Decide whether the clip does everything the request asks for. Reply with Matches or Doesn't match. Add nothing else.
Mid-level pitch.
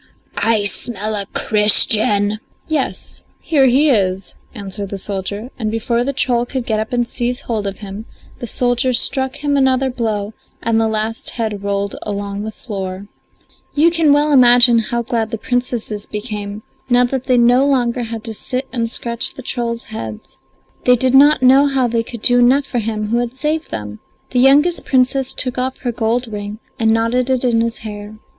Doesn't match